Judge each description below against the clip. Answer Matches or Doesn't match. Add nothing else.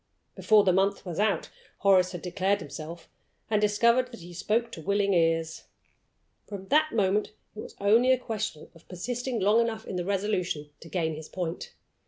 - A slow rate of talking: Doesn't match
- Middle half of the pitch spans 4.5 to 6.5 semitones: Doesn't match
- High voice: Matches